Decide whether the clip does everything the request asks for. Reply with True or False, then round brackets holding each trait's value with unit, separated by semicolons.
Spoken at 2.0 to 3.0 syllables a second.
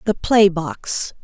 True (2.9 syllables/s)